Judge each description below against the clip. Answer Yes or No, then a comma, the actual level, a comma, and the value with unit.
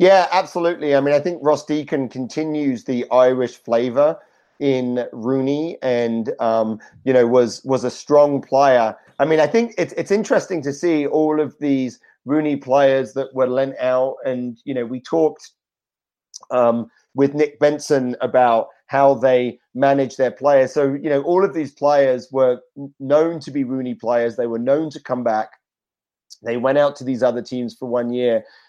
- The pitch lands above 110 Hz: Yes, low, 135 Hz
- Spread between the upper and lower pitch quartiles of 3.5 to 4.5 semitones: No, average, 3.0 semitones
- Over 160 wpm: Yes, average, 180 wpm